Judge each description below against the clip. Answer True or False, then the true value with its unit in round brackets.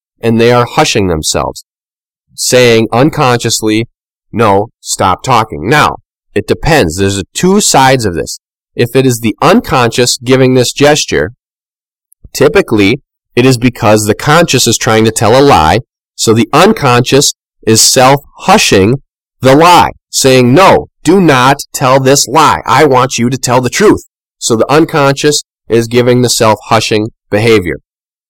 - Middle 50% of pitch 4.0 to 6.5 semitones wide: False (3.3 semitones)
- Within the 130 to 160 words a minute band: True (150 wpm)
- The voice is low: True (120 Hz)